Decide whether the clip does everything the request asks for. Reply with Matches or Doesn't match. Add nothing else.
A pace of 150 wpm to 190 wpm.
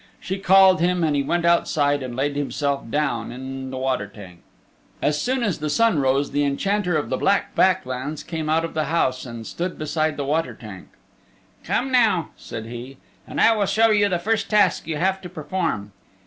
Doesn't match